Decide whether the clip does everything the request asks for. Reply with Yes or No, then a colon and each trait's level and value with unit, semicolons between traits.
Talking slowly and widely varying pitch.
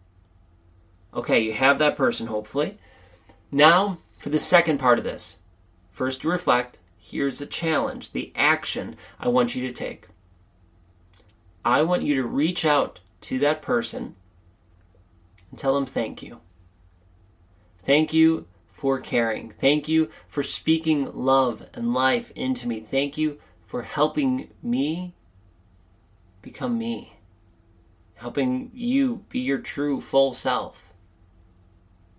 Yes: slow, 125 wpm; wide, 8.9 semitones